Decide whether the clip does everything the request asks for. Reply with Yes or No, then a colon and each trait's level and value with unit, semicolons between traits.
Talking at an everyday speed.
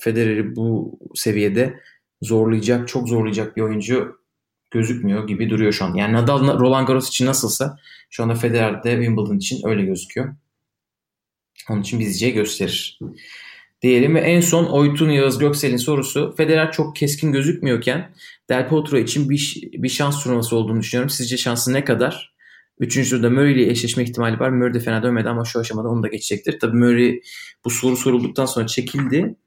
No: fast, 165 wpm